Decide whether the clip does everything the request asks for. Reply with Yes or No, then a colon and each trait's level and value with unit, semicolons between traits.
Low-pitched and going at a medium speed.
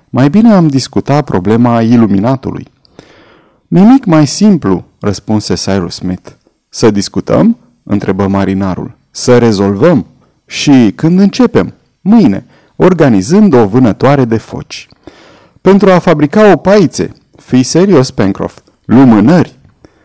No: low, 130 Hz; slow, 110 wpm